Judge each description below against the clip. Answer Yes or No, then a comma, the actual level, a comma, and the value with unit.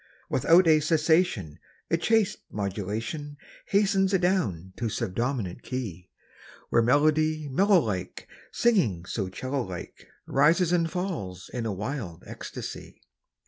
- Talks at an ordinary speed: No, slow, 115 wpm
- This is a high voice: No, low, 135 Hz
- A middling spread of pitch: No, wide, 8.9 semitones